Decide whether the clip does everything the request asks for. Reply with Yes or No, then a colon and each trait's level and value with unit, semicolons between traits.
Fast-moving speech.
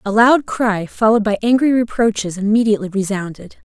No: average, 145 wpm